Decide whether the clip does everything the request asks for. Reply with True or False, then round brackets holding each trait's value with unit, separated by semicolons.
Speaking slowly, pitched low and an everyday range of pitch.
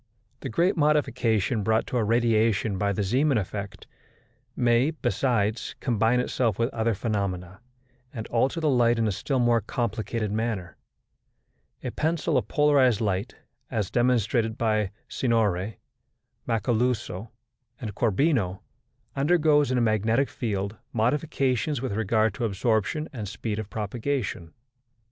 True (130 wpm; 115 Hz; 3.4 semitones)